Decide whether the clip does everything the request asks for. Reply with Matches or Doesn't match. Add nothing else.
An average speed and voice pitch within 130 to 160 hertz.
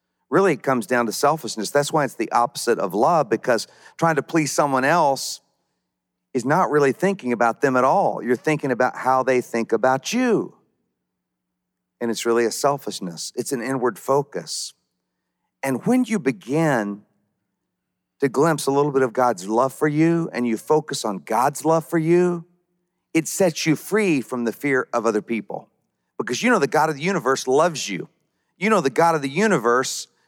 Matches